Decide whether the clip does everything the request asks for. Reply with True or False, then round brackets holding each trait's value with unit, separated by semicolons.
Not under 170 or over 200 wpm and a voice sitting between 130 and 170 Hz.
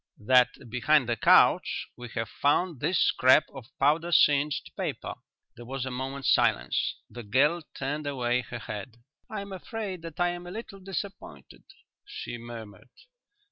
False (155 wpm; 140 Hz)